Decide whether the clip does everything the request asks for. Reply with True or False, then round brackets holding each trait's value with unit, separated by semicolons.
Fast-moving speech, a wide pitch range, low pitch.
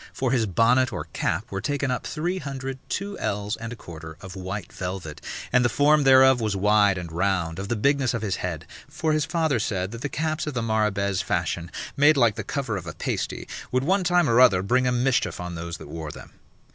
True (225 wpm; 6.1 semitones; 115 Hz)